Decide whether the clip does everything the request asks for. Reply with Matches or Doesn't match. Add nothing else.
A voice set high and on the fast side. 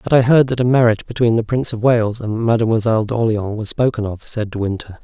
Doesn't match